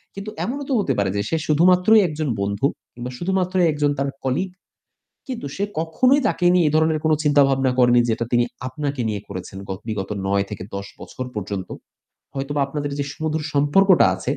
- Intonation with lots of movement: Yes, wide, 6.2 semitones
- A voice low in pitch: No, medium, 145 Hz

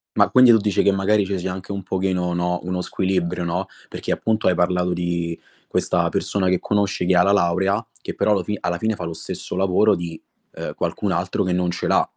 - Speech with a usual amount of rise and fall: No, narrow, 2.0 semitones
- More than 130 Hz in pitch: No, very low, 90 Hz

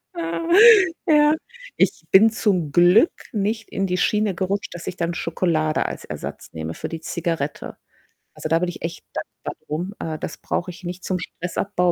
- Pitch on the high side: No, medium, 180 Hz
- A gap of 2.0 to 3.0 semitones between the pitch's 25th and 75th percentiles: No, average, 3.6 semitones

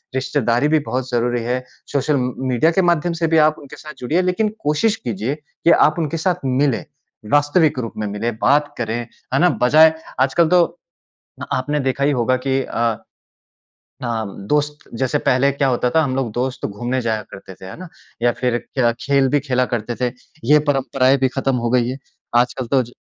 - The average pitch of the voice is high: No, low, 135 Hz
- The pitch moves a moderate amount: Yes, average, 3.4 semitones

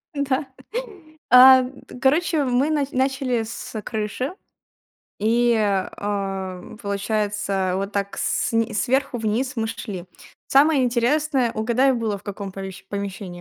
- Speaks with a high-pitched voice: Yes, high, 225 Hz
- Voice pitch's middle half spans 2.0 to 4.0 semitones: No, average, 4.6 semitones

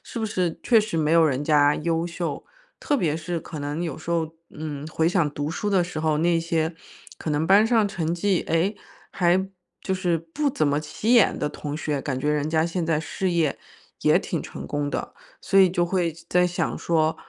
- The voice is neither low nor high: Yes, medium, 165 Hz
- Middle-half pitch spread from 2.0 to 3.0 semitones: Yes, average, 2.7 semitones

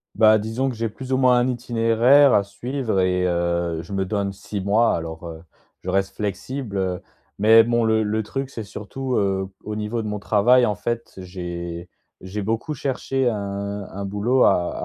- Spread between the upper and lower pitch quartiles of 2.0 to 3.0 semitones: No, average, 3.6 semitones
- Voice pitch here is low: Yes, low, 105 Hz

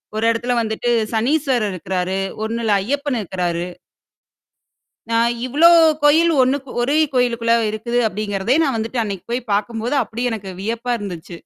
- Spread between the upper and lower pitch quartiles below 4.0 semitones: Yes, average, 3.4 semitones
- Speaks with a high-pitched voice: Yes, high, 230 Hz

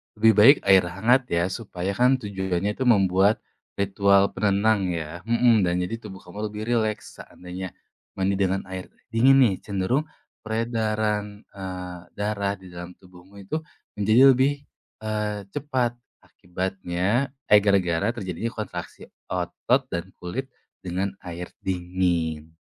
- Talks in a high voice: No, low, 100 Hz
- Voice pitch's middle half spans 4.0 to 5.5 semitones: No, average, 3.3 semitones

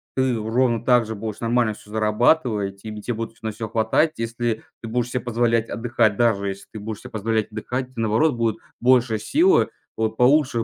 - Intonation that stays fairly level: Yes, narrow, 2.1 semitones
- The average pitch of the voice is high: No, low, 115 Hz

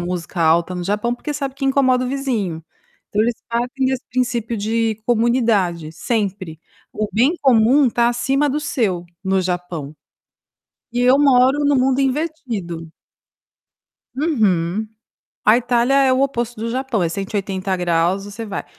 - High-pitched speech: Yes, high, 230 Hz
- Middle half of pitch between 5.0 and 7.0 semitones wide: Yes, wide, 5.5 semitones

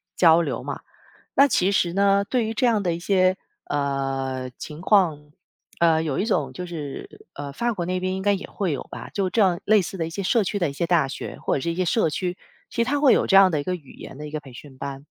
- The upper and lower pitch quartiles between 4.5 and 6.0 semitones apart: Yes, average, 5.0 semitones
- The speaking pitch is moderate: Yes, medium, 175 Hz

